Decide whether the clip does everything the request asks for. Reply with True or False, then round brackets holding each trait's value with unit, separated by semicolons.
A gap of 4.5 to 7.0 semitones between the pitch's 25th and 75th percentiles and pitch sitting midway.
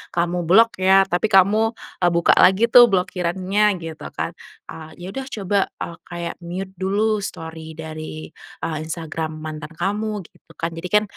False (3.6 semitones; 180 Hz)